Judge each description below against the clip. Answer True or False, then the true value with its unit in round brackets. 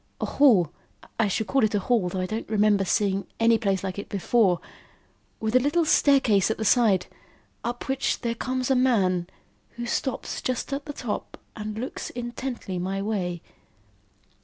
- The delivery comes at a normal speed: True (175 wpm)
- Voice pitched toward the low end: False (220 Hz)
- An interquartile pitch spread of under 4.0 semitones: False (4.3 semitones)